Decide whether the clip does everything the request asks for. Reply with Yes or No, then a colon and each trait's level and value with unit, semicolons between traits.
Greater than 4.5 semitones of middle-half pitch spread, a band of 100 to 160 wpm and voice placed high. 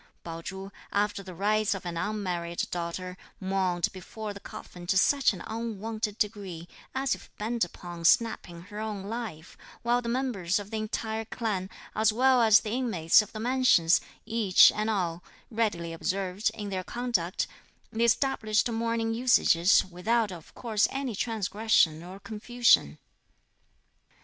No: average, 3.8 semitones; average, 150 wpm; high, 210 Hz